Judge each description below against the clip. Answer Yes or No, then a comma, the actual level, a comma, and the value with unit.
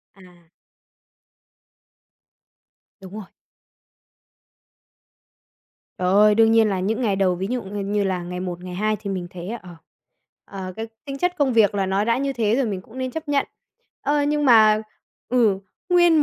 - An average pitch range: Yes, average, 4.8 semitones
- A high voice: Yes, high, 215 Hz